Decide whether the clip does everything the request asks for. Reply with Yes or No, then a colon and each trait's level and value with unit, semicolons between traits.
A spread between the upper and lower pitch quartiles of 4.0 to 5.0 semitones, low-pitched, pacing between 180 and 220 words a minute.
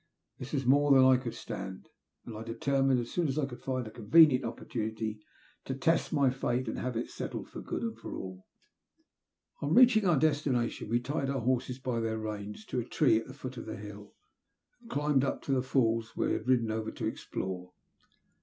No: average, 3.6 semitones; low, 125 Hz; fast, 205 wpm